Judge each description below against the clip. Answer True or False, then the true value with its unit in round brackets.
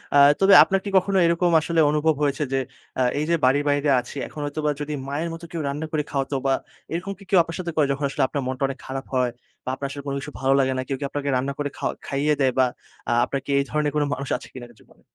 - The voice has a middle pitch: True (145 Hz)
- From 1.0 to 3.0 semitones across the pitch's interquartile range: True (2.7 semitones)